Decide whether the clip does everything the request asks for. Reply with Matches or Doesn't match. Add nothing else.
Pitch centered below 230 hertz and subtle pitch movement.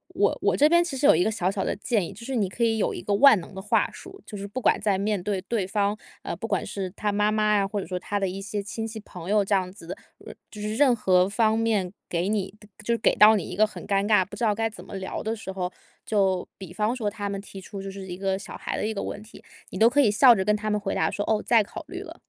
Matches